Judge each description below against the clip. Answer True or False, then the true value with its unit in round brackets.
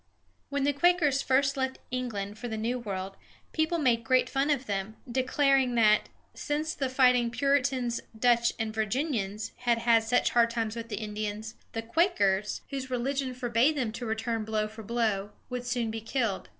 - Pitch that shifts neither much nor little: True (3.3 semitones)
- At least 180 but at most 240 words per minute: False (170 wpm)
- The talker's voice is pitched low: False (240 Hz)